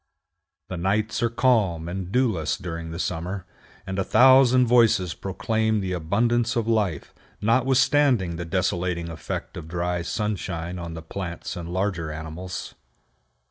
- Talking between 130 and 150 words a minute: Yes, average, 140 wpm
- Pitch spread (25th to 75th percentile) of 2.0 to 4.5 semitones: No, average, 5.0 semitones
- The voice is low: Yes, very low, 95 Hz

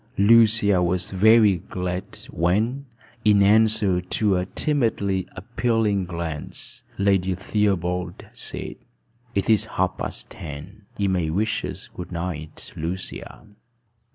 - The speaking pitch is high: No, very low, 95 Hz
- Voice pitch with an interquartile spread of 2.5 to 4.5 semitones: Yes, average, 3.1 semitones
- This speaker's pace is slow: Yes, slow, 115 wpm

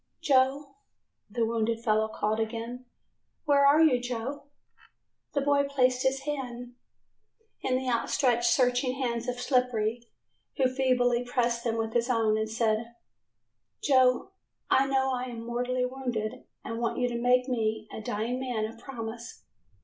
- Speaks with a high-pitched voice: Yes, high, 245 Hz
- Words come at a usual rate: Yes, average, 150 wpm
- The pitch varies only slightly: Yes, narrow, 2.1 semitones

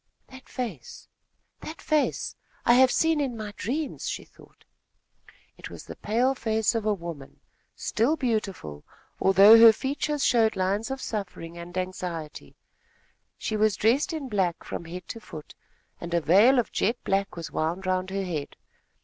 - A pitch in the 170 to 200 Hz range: No, high, 210 Hz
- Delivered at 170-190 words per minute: No, average, 160 wpm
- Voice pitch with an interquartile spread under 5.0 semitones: No, wide, 5.5 semitones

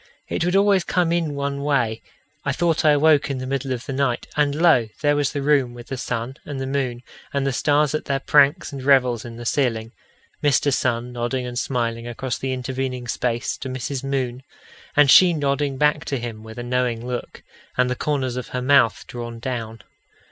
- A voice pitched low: Yes, low, 130 Hz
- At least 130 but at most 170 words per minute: No, fast, 205 wpm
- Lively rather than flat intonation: No, average, 2.9 semitones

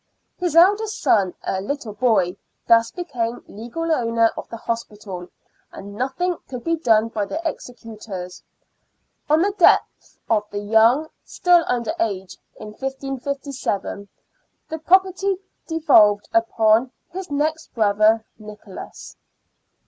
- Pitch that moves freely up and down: Yes, wide, 7.0 semitones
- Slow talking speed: Yes, slow, 120 wpm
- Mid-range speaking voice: No, high, 230 Hz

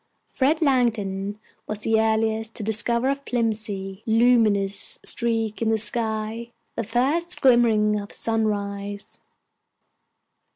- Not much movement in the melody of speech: Yes, narrow, 2.1 semitones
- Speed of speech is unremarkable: No, slow, 110 wpm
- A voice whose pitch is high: Yes, high, 220 Hz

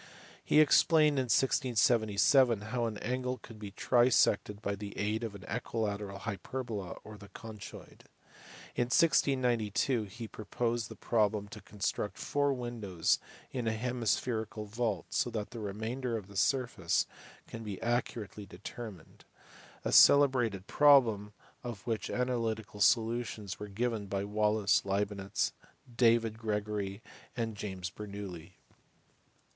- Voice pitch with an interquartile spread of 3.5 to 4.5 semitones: No, average, 3.0 semitones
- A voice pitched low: Yes, low, 110 Hz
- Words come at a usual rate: No, slow, 130 wpm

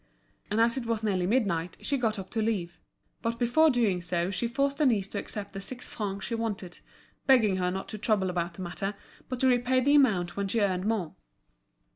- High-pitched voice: Yes, high, 215 Hz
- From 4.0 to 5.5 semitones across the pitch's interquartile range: Yes, average, 4.3 semitones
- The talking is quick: Yes, fast, 210 wpm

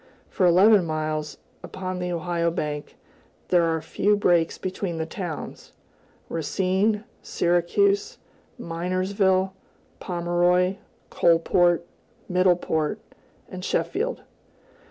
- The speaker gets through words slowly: Yes, slow, 90 wpm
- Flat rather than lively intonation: Yes, narrow, 2.2 semitones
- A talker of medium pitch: Yes, medium, 175 Hz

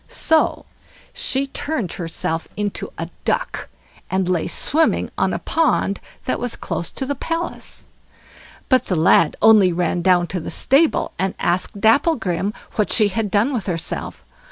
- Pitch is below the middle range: No, high, 205 Hz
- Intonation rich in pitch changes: Yes, wide, 6.8 semitones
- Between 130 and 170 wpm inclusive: Yes, average, 155 wpm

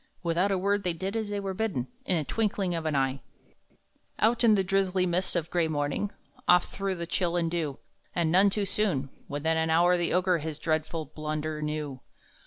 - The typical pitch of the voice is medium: Yes, medium, 175 Hz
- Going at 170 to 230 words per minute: Yes, average, 200 wpm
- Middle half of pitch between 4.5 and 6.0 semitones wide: No, average, 3.8 semitones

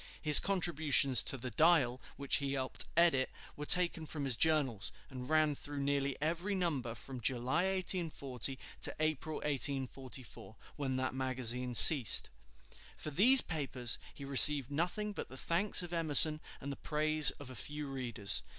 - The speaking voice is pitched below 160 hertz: Yes, medium, 140 Hz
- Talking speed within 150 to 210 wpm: Yes, average, 155 wpm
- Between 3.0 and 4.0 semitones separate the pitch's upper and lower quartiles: Yes, average, 3.3 semitones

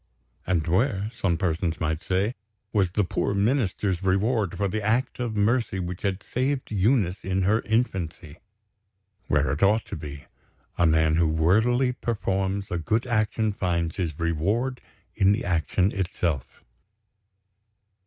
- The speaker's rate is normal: Yes, average, 145 wpm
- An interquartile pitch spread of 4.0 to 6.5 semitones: Yes, average, 4.3 semitones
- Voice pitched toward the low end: Yes, very low, 95 Hz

